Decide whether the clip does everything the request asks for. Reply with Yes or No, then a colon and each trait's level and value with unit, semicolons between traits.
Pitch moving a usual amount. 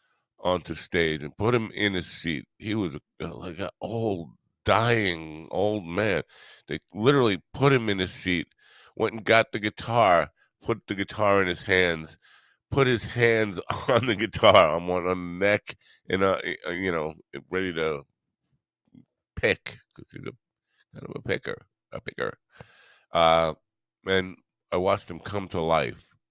Yes: average, 4.2 semitones